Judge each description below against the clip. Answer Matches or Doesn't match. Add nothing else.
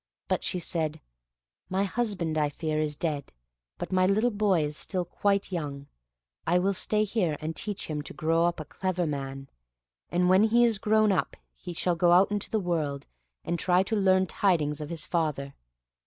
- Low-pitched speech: Doesn't match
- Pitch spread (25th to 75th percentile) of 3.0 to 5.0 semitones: Matches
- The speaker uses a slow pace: Doesn't match